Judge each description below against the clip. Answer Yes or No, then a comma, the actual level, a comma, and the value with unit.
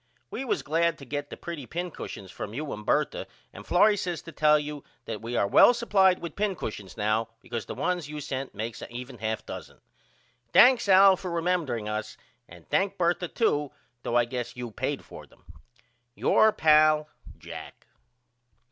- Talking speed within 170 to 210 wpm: Yes, average, 175 wpm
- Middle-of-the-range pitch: Yes, medium, 150 Hz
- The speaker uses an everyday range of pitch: No, wide, 7.1 semitones